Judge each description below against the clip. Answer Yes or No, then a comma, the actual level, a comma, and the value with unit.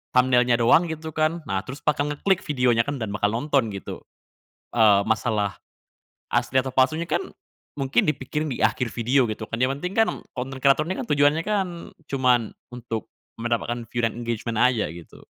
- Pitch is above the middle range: No, low, 125 Hz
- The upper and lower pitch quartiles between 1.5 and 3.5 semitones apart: No, average, 4.1 semitones